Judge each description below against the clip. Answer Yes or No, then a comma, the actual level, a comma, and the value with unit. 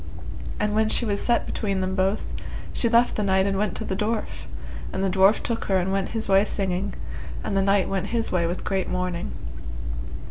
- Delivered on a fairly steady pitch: Yes, narrow, 2.0 semitones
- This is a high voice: Yes, high, 195 Hz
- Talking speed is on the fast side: Yes, fast, 210 wpm